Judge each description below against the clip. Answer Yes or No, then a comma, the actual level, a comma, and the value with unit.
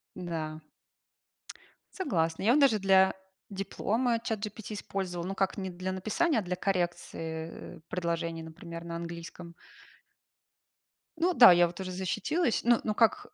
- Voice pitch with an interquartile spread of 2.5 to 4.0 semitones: No, average, 4.5 semitones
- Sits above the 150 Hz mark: Yes, high, 190 Hz